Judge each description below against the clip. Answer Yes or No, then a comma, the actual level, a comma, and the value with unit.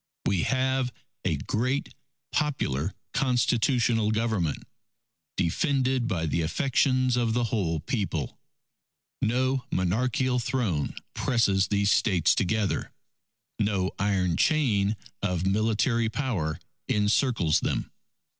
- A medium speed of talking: No, slow, 100 wpm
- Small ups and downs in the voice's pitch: No, average, 5.1 semitones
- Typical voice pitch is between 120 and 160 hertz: No, low, 110 Hz